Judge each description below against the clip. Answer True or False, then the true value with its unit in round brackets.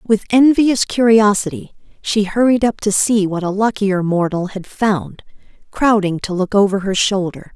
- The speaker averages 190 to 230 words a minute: False (160 wpm)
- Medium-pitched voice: False (205 Hz)